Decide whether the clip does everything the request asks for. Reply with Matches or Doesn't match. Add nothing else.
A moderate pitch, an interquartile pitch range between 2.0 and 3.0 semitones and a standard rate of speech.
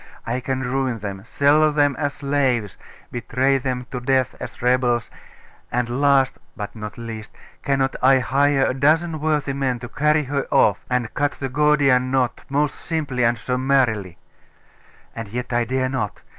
Doesn't match